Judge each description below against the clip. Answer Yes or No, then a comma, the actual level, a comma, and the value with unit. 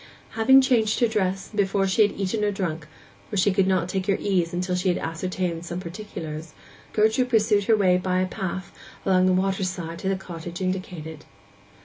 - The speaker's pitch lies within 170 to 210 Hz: Yes, medium, 185 Hz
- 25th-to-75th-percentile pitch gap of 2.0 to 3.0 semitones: Yes, narrow, 2.4 semitones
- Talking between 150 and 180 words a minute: No, average, 190 wpm